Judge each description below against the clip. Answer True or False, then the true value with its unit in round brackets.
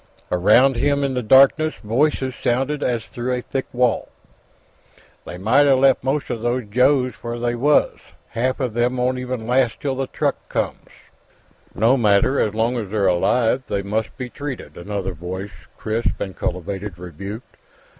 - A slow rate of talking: False (160 wpm)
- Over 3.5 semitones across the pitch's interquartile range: True (3.9 semitones)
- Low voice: True (120 Hz)